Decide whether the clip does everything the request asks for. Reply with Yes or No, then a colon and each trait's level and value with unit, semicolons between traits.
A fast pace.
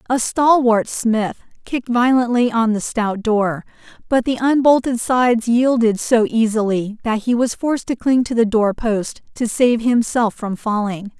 No: average, 165 wpm